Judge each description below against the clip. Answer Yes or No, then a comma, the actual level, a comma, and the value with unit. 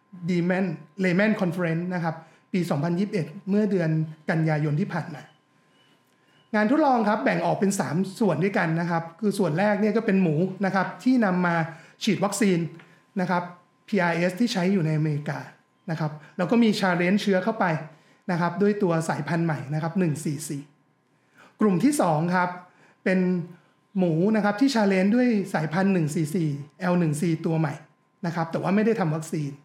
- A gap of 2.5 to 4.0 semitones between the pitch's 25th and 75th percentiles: Yes, average, 3.4 semitones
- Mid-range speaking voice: Yes, medium, 180 Hz